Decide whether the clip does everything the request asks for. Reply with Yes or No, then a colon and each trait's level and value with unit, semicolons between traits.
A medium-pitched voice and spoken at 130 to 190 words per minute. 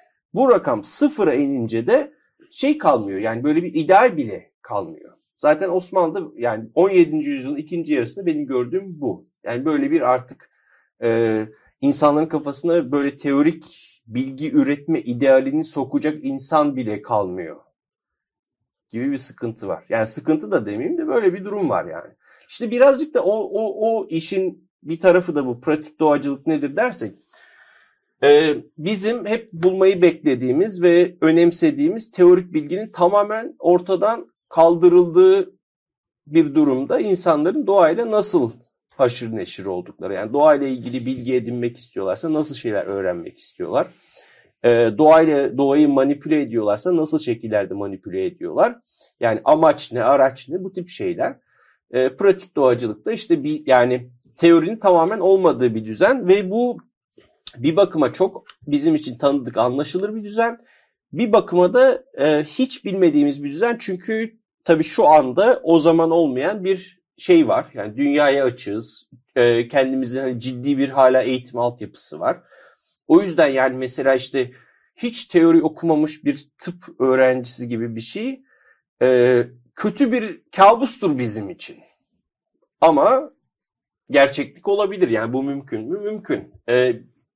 Yes: medium, 160 Hz; average, 135 wpm